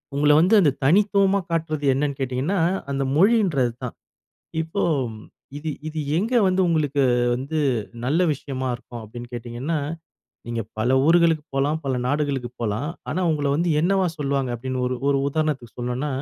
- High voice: No, medium, 145 Hz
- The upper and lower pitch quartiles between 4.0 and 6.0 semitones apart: Yes, average, 4.3 semitones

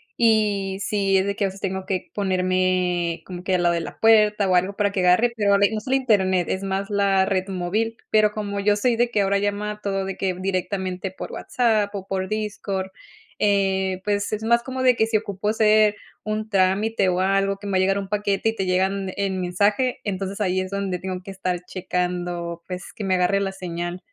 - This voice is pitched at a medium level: No, high, 195 Hz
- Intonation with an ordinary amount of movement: No, narrow, 2.0 semitones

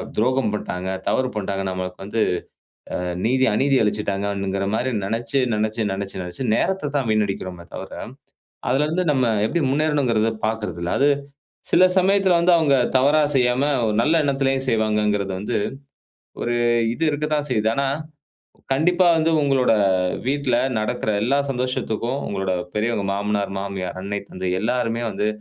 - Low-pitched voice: Yes, low, 115 Hz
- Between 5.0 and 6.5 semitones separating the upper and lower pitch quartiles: Yes, wide, 5.4 semitones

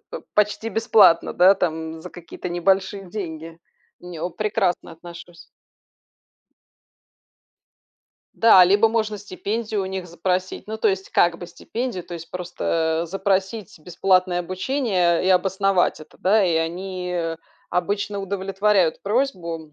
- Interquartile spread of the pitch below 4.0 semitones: Yes, average, 2.8 semitones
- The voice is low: No, medium, 185 Hz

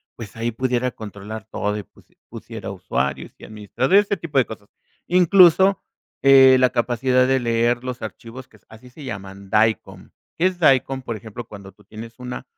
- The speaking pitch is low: Yes, low, 120 Hz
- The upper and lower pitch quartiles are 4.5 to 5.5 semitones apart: No, average, 3.4 semitones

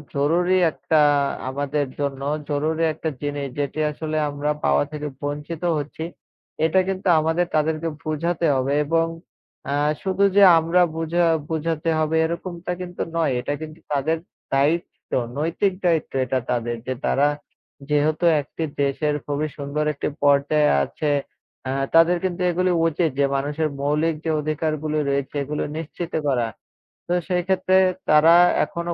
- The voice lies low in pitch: No, medium, 155 Hz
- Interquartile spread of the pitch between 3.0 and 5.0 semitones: No, narrow, 2.5 semitones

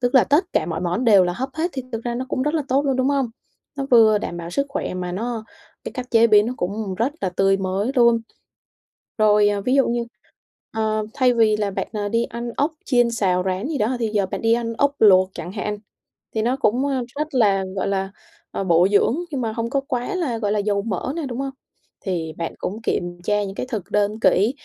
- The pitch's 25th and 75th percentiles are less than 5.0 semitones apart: Yes, average, 4.3 semitones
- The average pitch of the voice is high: Yes, high, 220 Hz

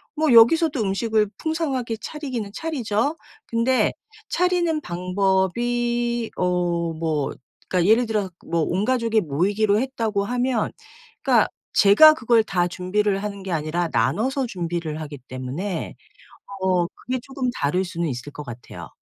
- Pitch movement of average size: No, wide, 5.7 semitones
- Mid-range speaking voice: No, high, 210 Hz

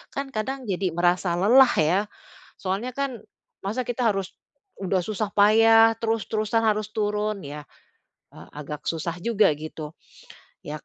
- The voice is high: Yes, high, 210 Hz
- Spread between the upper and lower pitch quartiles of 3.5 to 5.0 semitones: Yes, average, 4.1 semitones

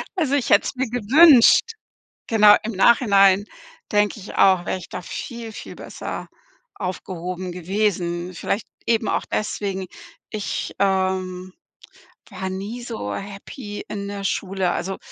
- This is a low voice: No, high, 200 Hz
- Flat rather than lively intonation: No, average, 3.0 semitones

